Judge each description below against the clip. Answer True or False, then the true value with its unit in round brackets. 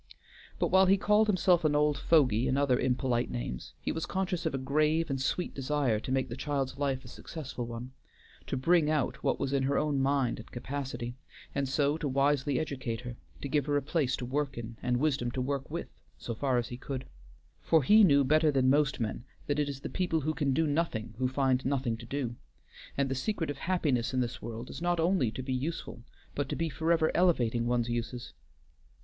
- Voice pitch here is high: False (140 Hz)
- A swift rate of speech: True (220 wpm)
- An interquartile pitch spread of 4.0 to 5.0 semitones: False (3.4 semitones)